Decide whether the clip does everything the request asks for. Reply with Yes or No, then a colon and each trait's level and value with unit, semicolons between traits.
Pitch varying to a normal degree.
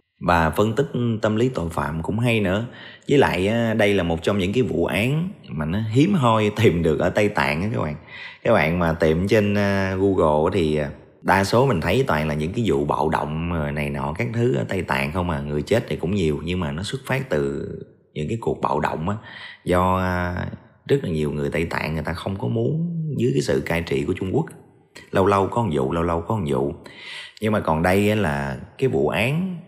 No: wide, 6.5 semitones